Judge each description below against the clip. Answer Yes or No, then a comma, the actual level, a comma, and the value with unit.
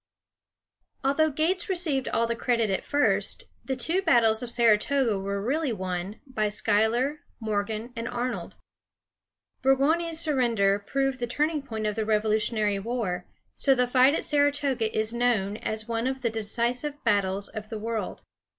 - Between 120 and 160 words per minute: Yes, average, 150 wpm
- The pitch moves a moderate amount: Yes, average, 4.1 semitones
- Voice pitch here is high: Yes, high, 235 Hz